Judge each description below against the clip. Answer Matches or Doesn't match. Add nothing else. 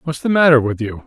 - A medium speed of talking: Doesn't match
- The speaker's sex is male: Matches